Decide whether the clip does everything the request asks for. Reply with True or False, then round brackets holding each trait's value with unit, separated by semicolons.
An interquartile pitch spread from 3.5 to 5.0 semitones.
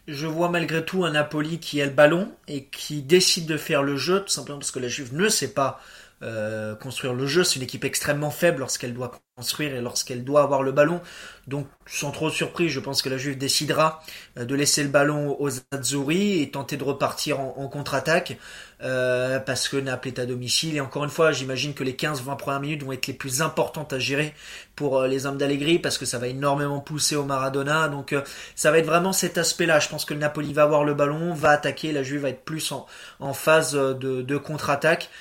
False (2.6 semitones)